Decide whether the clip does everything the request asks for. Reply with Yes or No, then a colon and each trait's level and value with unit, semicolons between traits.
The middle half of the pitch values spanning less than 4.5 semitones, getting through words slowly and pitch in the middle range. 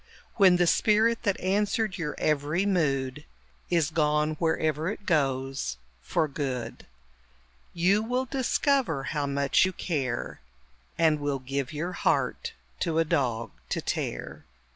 No: average, 5.1 semitones; slow, 130 wpm; medium, 155 Hz